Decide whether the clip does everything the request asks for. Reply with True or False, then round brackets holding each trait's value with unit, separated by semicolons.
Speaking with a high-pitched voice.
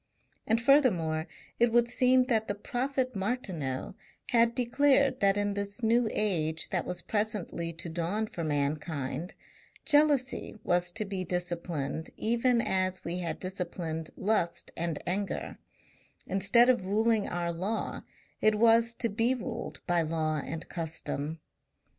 True (195 Hz)